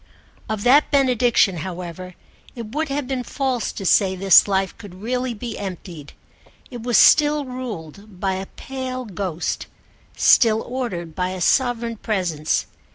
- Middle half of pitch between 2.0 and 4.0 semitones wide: No, wide, 5.4 semitones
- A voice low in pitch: No, high, 215 Hz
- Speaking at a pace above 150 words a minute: No, average, 145 wpm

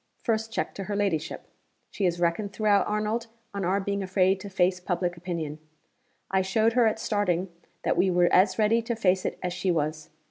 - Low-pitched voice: No, high, 190 Hz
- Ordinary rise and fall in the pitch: Yes, average, 3.0 semitones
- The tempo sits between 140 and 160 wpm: No, average, 200 wpm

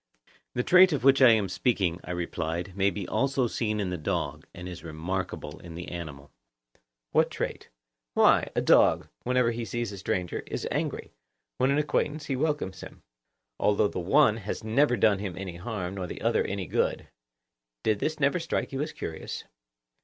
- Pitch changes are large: Yes, wide, 6.4 semitones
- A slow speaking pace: No, average, 185 wpm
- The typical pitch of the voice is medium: No, low, 100 Hz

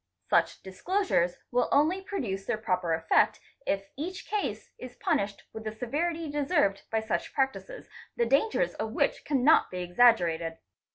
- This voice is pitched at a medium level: No, high, 240 Hz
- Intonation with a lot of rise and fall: Yes, wide, 8.6 semitones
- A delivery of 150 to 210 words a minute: Yes, average, 155 wpm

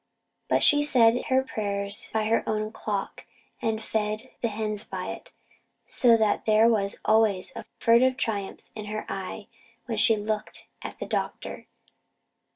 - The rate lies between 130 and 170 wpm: Yes, average, 155 wpm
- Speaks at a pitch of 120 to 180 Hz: No, high, 220 Hz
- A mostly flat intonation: Yes, narrow, 1.5 semitones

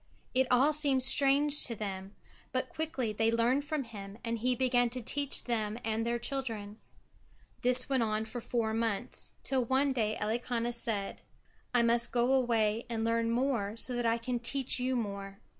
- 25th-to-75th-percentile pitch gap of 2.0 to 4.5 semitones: Yes, narrow, 2.6 semitones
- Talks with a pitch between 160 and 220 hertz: No, high, 235 Hz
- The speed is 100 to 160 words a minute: No, average, 175 wpm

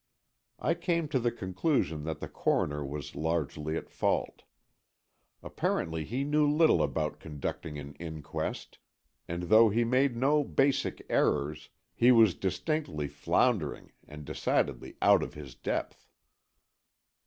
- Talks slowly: Yes, slow, 130 wpm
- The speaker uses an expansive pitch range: Yes, wide, 9.0 semitones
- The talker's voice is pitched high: No, very low, 85 Hz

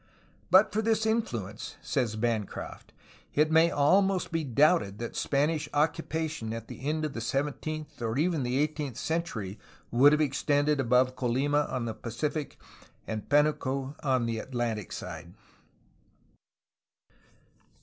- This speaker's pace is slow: Yes, slow, 130 wpm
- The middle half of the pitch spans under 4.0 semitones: No, average, 4.7 semitones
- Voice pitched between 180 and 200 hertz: No, medium, 140 Hz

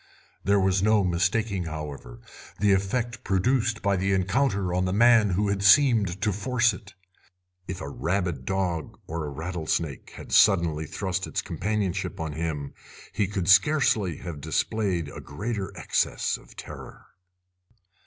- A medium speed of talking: Yes, average, 145 wpm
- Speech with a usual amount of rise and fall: Yes, average, 3.6 semitones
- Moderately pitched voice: No, very low, 95 Hz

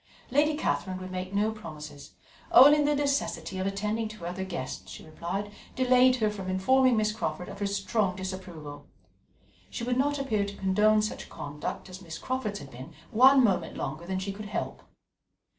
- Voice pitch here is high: Yes, high, 200 Hz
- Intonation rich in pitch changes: No, average, 4.7 semitones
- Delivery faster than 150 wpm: Yes, average, 180 wpm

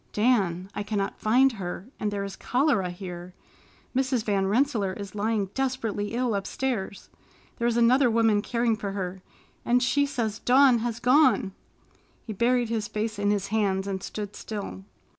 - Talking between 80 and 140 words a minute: No, average, 160 wpm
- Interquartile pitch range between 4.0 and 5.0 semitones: No, average, 3.6 semitones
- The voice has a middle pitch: No, high, 215 Hz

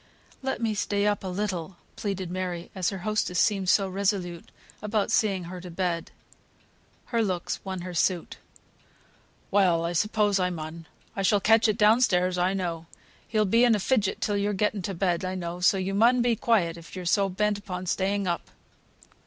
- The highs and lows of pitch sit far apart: No, average, 2.7 semitones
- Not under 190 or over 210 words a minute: Yes, average, 195 wpm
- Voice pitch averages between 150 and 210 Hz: Yes, high, 190 Hz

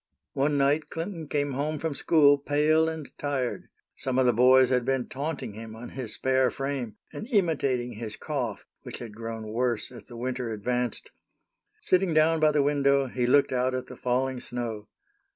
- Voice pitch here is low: Yes, low, 130 Hz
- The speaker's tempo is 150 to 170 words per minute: No, average, 180 wpm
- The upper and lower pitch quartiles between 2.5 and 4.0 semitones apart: Yes, average, 3.1 semitones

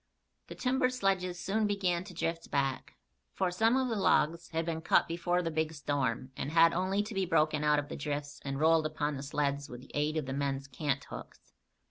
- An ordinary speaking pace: No, fast, 210 wpm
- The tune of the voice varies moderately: Yes, average, 4.1 semitones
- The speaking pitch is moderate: Yes, medium, 160 Hz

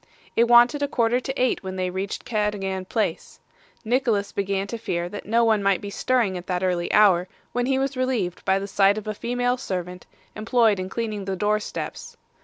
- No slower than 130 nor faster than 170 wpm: No, fast, 205 wpm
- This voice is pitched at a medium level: No, high, 210 Hz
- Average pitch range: Yes, average, 4.0 semitones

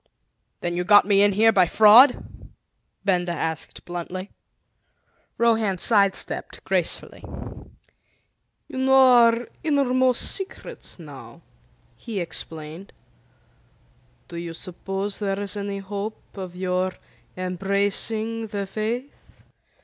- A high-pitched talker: Yes, high, 200 Hz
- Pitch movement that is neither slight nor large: Yes, average, 3.7 semitones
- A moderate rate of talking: No, slow, 105 wpm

